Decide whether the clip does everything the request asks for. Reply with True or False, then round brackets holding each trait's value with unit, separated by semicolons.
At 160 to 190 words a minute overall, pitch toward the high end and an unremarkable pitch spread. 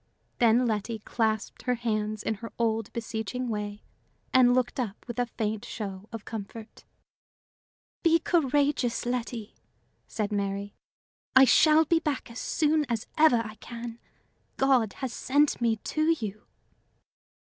False (135 wpm; 235 Hz; 3.1 semitones)